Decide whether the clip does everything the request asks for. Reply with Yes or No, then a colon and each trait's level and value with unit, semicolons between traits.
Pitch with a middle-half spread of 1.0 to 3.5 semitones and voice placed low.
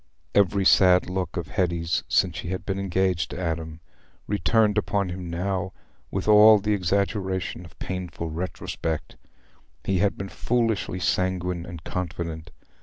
Yes: narrow, 2.4 semitones; very low, 90 Hz